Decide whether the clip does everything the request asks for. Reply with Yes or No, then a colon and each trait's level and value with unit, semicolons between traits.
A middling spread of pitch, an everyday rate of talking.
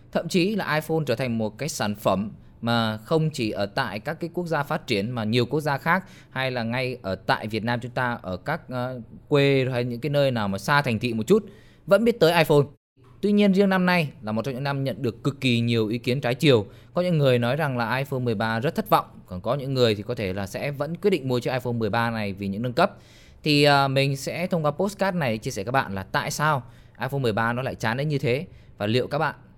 No: average, 4.5 semitones; fast, 265 wpm